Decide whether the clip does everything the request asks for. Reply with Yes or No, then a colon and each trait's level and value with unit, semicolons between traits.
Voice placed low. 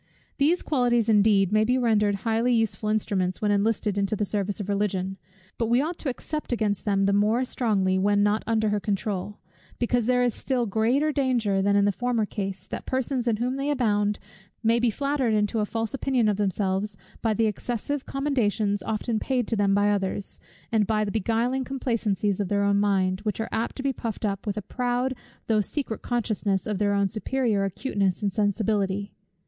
No: high, 215 Hz